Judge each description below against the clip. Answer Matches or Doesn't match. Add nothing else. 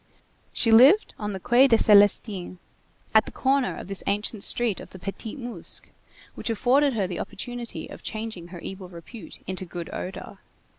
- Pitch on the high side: Matches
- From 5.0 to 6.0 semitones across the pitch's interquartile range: Doesn't match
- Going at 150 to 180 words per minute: Matches